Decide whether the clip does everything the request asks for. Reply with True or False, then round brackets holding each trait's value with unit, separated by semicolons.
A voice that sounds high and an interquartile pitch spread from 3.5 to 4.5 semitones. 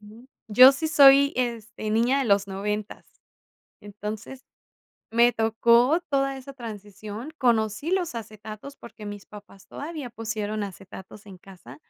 True (225 Hz; 4.1 semitones)